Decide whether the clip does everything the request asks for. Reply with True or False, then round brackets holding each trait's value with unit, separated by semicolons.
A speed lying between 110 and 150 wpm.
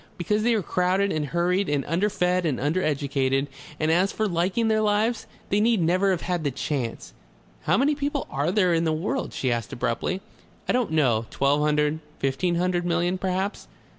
False (185 wpm)